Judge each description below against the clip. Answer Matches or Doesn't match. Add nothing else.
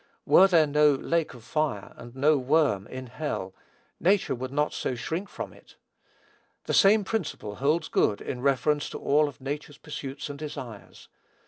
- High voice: Doesn't match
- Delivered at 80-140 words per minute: Doesn't match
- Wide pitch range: Doesn't match